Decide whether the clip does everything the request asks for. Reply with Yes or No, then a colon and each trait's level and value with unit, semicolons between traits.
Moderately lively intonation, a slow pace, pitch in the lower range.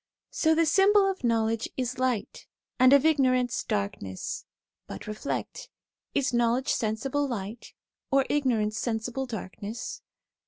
No: average, 4.0 semitones; slow, 125 wpm; very high, 250 Hz